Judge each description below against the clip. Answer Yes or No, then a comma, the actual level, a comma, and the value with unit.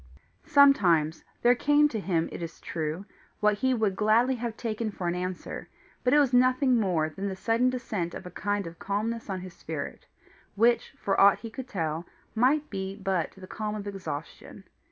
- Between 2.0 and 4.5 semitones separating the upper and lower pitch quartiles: No, average, 4.9 semitones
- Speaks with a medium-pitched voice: No, high, 205 Hz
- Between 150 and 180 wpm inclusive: No, average, 190 wpm